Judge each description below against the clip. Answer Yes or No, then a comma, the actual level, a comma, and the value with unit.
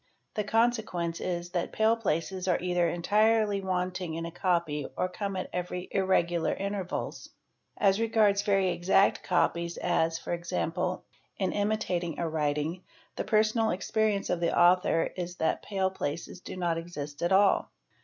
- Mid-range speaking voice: Yes, medium, 180 Hz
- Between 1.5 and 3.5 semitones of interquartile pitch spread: Yes, average, 2.7 semitones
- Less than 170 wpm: Yes, average, 150 wpm